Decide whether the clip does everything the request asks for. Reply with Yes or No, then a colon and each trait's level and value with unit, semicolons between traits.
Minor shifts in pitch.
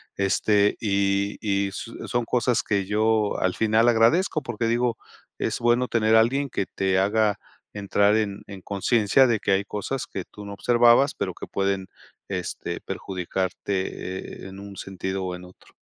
No: average, 3.0 semitones